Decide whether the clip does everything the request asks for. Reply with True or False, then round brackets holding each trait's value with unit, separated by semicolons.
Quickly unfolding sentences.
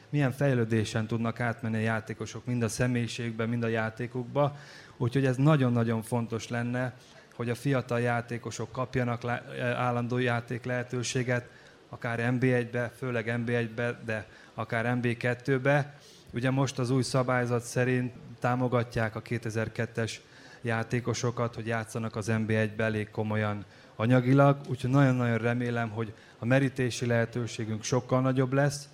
False (125 wpm)